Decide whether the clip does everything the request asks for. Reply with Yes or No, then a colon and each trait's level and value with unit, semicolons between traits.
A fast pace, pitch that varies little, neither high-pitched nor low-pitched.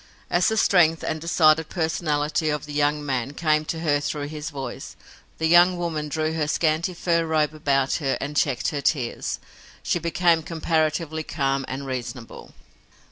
No: average, 165 wpm; narrow, 2.1 semitones; medium, 155 Hz